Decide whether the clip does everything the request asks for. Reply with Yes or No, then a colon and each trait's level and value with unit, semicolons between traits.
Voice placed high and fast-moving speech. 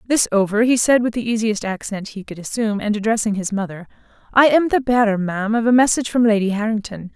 Yes: high, 220 Hz; fast, 220 wpm